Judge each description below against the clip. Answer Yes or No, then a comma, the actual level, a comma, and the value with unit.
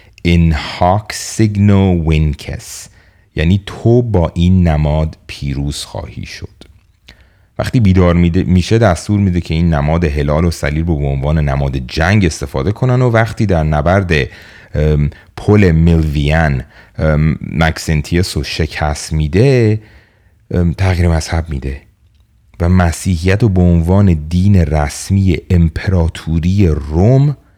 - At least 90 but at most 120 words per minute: Yes, average, 115 wpm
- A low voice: Yes, very low, 90 Hz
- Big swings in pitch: No, average, 3.9 semitones